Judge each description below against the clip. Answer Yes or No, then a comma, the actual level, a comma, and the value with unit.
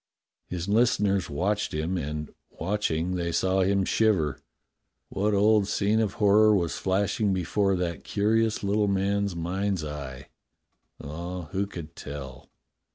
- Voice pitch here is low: Yes, very low, 95 Hz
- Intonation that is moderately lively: Yes, average, 3.3 semitones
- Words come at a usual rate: No, slow, 130 wpm